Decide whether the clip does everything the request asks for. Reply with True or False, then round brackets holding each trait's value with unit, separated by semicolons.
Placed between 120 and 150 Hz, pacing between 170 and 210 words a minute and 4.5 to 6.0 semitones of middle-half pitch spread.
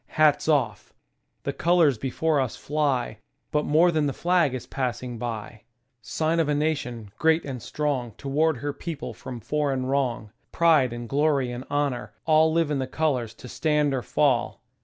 False (140 Hz; 190 wpm; 3.9 semitones)